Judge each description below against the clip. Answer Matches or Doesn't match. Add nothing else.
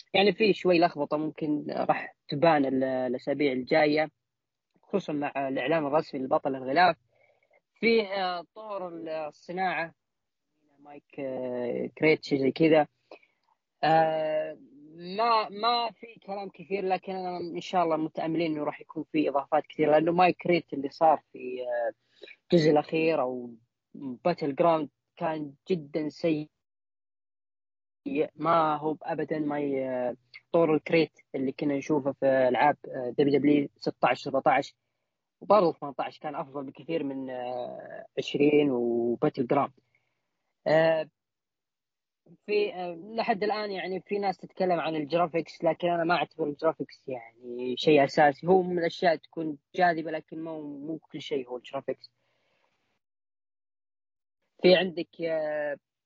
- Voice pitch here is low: Doesn't match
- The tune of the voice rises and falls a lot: Doesn't match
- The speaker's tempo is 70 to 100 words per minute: Doesn't match